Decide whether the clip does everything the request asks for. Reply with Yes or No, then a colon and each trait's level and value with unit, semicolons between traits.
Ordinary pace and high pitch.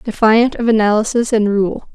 Yes: average, 155 wpm; high, 220 Hz